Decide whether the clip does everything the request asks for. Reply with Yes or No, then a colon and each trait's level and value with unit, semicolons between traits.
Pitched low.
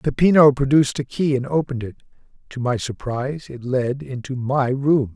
Yes: low, 130 Hz